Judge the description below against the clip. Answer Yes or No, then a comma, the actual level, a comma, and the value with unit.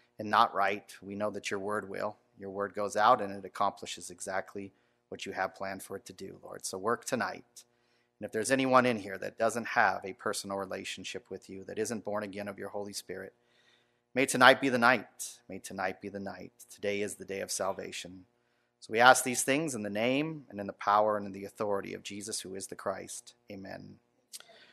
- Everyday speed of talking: No, fast, 220 wpm